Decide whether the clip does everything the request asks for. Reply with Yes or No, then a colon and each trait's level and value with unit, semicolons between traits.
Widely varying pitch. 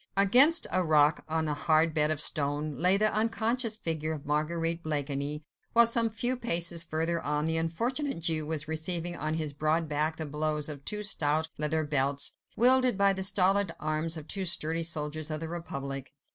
No: average, 3.9 semitones